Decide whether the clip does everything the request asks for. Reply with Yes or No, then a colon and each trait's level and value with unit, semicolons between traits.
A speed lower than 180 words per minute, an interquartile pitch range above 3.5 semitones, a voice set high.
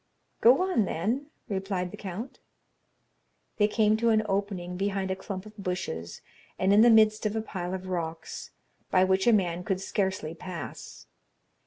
No: average, 165 wpm; average, 2.9 semitones; high, 195 Hz